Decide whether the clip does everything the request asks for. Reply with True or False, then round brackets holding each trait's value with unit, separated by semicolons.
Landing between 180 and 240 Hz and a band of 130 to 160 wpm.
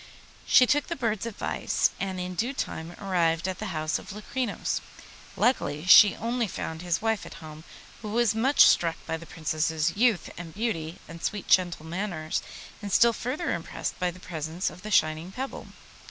False (185 Hz; 180 wpm)